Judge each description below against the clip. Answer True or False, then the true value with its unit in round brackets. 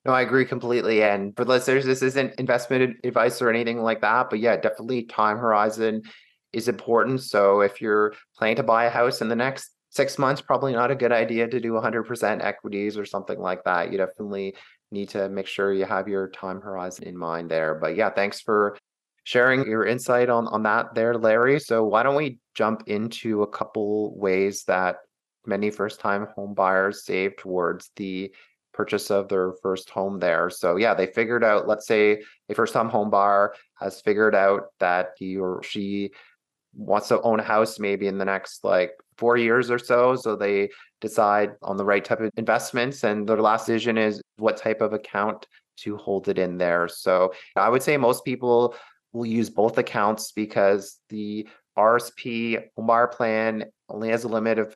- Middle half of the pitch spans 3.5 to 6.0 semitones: False (2.8 semitones)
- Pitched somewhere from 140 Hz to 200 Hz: False (110 Hz)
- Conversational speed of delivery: True (190 wpm)